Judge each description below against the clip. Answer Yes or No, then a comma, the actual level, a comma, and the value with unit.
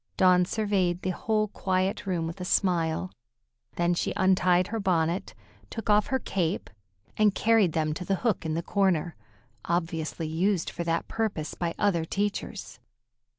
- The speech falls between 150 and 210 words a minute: Yes, average, 155 wpm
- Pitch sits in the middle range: Yes, medium, 180 Hz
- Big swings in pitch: No, average, 3.1 semitones